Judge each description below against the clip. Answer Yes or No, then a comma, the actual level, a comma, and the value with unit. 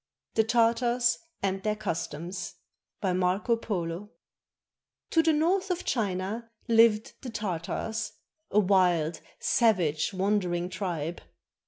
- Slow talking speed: Yes, slow, 110 wpm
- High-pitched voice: Yes, high, 205 Hz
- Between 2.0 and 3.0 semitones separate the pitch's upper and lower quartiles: No, average, 4.2 semitones